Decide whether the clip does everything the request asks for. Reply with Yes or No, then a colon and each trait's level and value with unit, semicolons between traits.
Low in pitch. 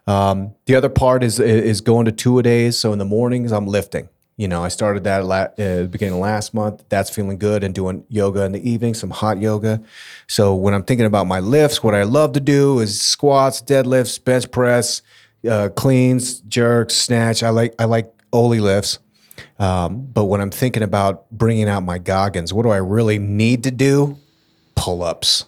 Yes: low, 110 Hz